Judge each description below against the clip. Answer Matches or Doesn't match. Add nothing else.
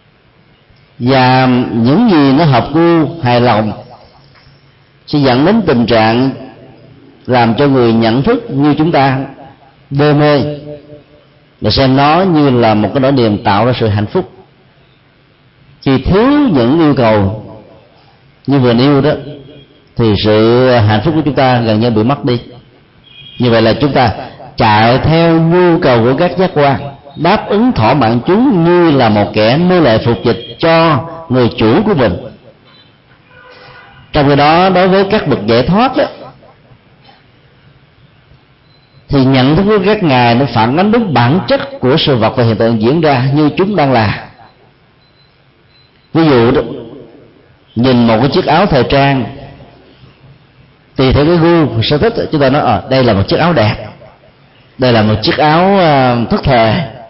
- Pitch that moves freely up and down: Doesn't match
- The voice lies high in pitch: Doesn't match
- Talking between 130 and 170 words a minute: Matches